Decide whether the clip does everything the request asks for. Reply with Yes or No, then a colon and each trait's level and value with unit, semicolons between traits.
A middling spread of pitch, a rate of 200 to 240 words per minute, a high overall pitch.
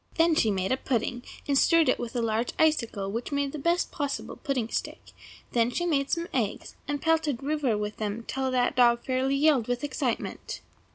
Yes: average, 3.9 semitones; fast, 205 wpm; very high, 260 Hz